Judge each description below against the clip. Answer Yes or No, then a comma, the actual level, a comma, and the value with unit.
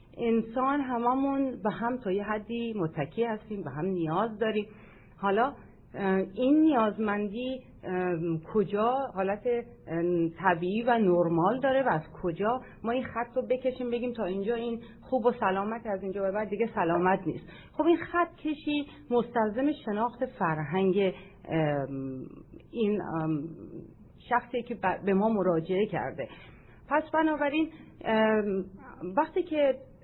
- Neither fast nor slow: Yes, average, 130 wpm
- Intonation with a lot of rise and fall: No, average, 4.9 semitones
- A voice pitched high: Yes, high, 215 Hz